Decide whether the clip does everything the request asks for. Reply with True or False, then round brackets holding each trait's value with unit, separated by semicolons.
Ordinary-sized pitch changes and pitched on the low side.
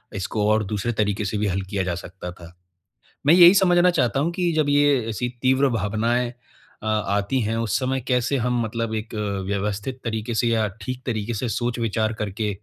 True (3.7 semitones; 115 Hz)